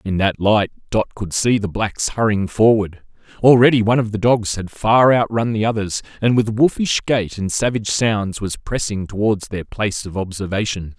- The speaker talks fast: No, average, 185 wpm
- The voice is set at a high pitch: No, low, 105 Hz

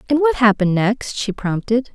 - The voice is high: Yes, high, 230 Hz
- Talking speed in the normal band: Yes, average, 185 wpm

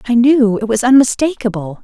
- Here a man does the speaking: No, female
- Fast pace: No, average, 165 wpm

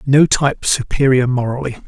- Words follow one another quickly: No, slow, 130 wpm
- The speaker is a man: Yes, male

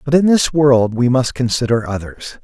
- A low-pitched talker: Yes, low, 130 Hz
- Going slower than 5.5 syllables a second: Yes, 5.0 syllables/s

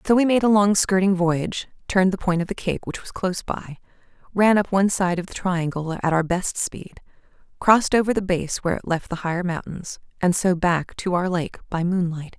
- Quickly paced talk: Yes, fast, 225 wpm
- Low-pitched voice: No, medium, 185 Hz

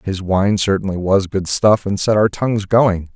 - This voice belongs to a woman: No, male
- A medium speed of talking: No, fast, 210 wpm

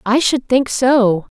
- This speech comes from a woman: Yes, female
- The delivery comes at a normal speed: Yes, average, 170 wpm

